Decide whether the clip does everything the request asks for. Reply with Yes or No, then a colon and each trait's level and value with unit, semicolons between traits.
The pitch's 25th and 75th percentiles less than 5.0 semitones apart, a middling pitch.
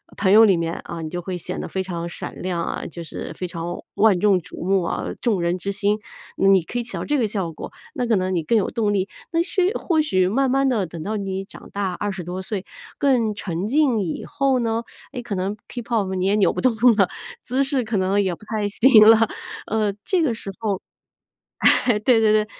No: average, 4.0 semitones; high, 205 Hz